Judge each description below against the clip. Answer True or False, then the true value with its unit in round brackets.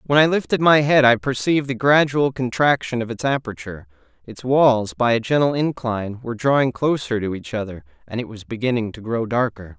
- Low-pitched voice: True (125 Hz)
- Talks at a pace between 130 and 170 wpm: False (195 wpm)